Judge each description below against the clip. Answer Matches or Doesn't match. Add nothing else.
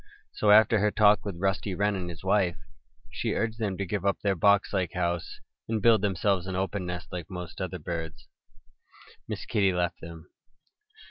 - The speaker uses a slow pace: Doesn't match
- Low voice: Matches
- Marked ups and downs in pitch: Doesn't match